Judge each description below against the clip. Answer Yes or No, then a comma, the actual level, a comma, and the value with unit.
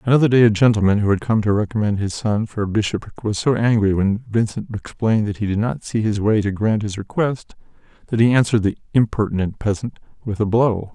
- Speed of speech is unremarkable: No, fast, 220 wpm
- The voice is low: Yes, low, 110 Hz